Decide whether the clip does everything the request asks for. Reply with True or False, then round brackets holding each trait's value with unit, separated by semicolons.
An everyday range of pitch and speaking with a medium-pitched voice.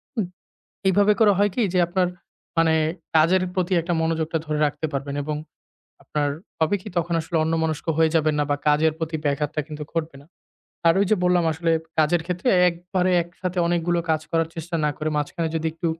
False (2.3 semitones; 165 Hz)